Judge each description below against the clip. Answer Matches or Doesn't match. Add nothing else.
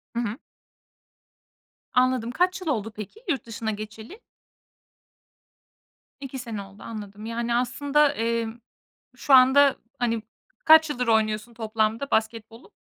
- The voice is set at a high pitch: Matches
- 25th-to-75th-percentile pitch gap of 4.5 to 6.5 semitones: Doesn't match